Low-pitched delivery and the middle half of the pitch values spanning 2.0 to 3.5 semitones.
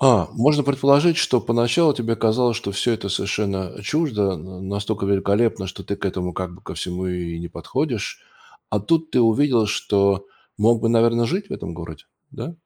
No: low, 105 Hz; average, 4.3 semitones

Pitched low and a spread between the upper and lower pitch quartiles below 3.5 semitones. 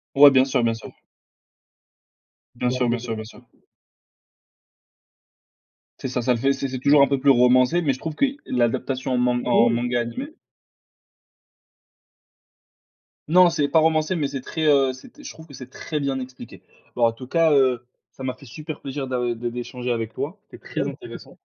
Yes: low, 130 Hz; average, 3.0 semitones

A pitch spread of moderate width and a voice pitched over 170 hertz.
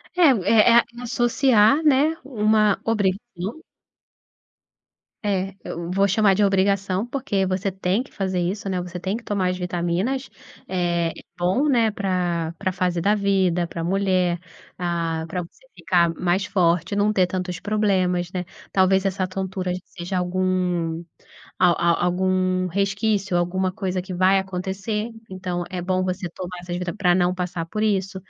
No: narrow, 2.1 semitones; medium, 185 Hz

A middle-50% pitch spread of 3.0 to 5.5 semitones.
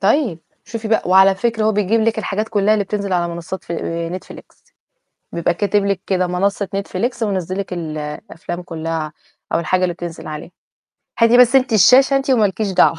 Yes: average, 4.1 semitones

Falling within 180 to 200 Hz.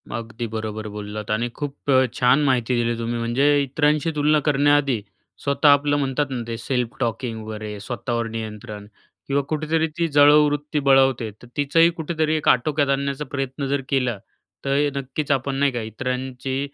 No: low, 135 Hz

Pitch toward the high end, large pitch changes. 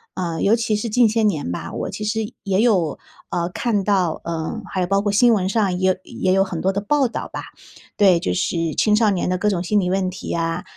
No: high, 195 Hz; average, 3.2 semitones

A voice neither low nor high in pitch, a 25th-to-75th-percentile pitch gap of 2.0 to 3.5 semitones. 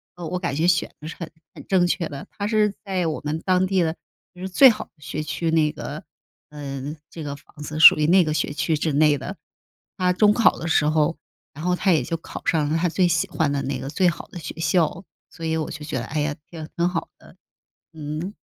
Yes: medium, 160 Hz; average, 3.0 semitones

